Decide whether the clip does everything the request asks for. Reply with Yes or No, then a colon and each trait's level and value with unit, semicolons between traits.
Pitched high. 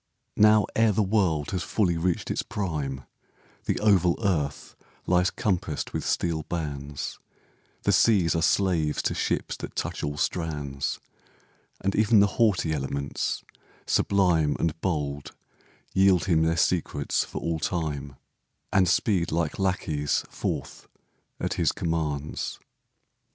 No: very low, 85 Hz